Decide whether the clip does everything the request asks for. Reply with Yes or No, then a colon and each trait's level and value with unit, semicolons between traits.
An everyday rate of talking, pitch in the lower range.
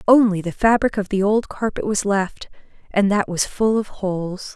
No: average, 185 wpm; high, 200 Hz